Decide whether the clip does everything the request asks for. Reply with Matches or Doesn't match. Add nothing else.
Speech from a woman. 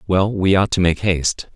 Doesn't match